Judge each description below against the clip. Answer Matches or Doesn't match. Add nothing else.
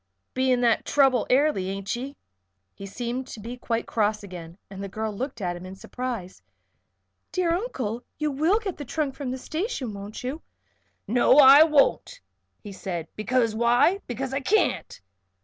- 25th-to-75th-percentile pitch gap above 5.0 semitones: Matches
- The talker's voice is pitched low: Doesn't match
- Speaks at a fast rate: Doesn't match